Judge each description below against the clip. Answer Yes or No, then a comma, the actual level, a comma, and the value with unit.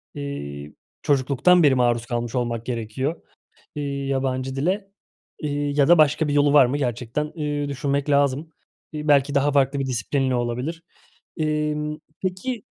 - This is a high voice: No, medium, 140 Hz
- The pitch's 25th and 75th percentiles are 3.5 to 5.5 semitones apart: No, average, 2.7 semitones